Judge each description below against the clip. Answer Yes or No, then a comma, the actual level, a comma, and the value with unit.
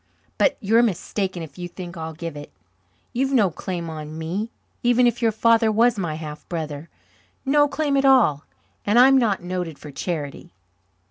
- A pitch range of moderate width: No, wide, 6.8 semitones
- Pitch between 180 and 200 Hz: Yes, high, 190 Hz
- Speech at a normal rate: Yes, average, 175 wpm